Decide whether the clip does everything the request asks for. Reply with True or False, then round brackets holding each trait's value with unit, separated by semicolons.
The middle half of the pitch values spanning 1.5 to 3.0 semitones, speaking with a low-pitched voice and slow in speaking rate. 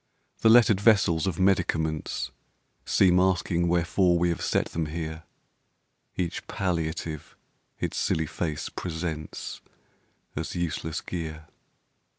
True (2.4 semitones; 85 Hz; 110 wpm)